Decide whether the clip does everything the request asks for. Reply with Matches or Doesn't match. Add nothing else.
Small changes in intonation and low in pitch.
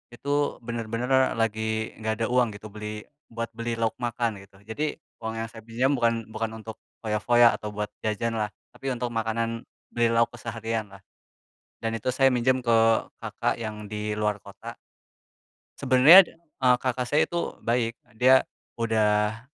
Matches